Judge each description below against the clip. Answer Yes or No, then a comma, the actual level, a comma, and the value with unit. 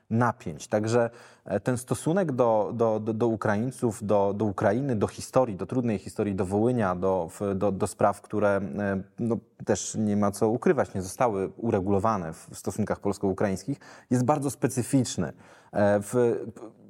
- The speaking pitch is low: Yes, low, 110 Hz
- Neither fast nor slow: Yes, average, 145 wpm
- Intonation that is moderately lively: Yes, average, 3.1 semitones